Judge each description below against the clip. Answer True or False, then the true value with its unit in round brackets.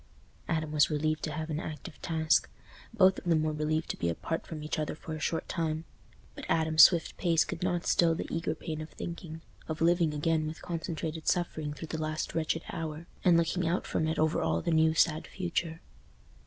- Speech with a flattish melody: True (1.2 semitones)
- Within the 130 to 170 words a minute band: False (200 wpm)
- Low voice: False (160 Hz)